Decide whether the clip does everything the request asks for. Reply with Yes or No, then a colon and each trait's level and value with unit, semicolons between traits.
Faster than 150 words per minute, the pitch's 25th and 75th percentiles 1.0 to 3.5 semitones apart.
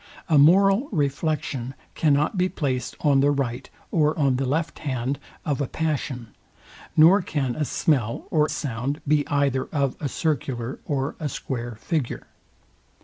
No: average, 145 wpm; average, 3.0 semitones